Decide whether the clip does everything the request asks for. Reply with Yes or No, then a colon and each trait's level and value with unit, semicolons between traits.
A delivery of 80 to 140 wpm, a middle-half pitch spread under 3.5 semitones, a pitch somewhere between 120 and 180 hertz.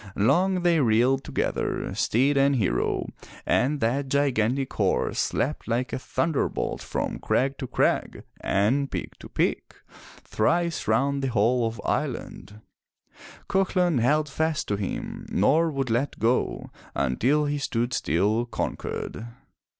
No: slow, 135 wpm; average, 4.4 semitones; low, 135 Hz